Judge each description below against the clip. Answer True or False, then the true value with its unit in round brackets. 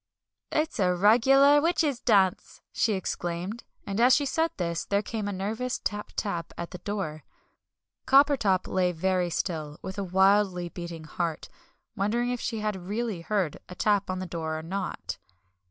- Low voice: False (195 Hz)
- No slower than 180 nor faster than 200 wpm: False (165 wpm)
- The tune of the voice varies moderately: True (4.3 semitones)